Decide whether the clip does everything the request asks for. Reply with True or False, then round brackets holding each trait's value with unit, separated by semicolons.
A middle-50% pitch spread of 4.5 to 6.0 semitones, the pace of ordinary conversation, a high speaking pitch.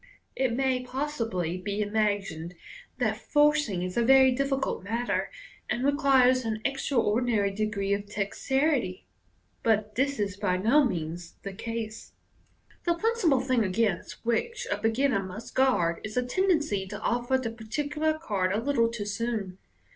True (4.9 semitones; 145 wpm; 230 Hz)